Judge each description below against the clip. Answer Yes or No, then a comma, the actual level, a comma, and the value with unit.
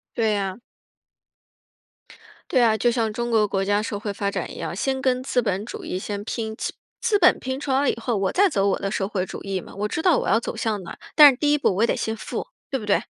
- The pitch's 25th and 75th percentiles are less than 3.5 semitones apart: No, average, 4.5 semitones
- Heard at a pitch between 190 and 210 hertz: No, high, 220 Hz